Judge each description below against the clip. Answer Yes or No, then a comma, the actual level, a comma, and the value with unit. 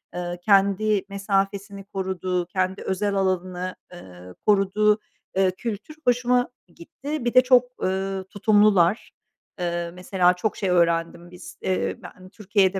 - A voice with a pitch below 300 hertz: Yes, high, 190 Hz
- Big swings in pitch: No, average, 2.7 semitones